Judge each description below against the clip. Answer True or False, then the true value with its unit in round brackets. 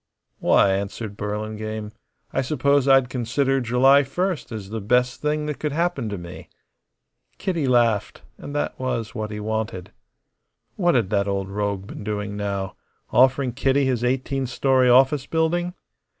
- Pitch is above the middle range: False (125 Hz)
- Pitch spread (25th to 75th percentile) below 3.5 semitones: False (4.6 semitones)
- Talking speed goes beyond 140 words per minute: True (150 wpm)